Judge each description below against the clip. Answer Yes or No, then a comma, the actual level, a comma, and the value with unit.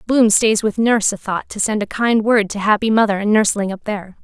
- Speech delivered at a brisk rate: Yes, fast, 255 wpm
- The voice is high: Yes, high, 210 Hz